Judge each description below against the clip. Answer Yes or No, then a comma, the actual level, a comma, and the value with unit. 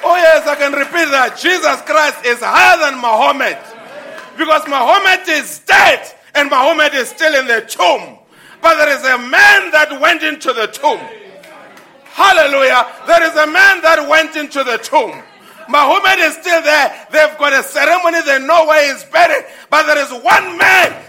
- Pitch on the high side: Yes, very high, 305 Hz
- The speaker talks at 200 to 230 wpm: No, average, 175 wpm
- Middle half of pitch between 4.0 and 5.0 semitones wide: No, average, 2.8 semitones